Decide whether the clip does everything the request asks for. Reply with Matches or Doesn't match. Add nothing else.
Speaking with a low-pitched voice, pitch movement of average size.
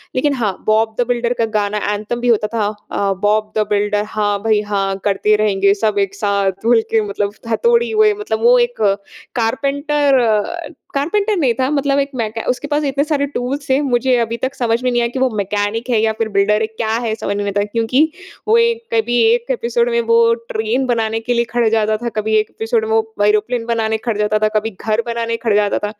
Doesn't match